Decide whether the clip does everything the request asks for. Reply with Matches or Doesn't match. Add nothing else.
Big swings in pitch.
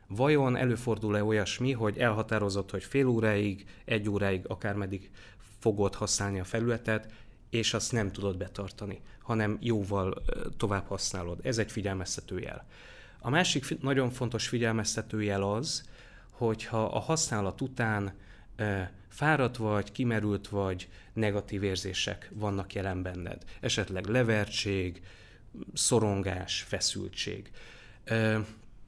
Doesn't match